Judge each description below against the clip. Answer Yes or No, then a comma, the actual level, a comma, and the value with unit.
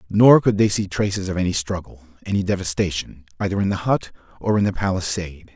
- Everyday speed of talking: Yes, average, 195 wpm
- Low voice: Yes, very low, 95 Hz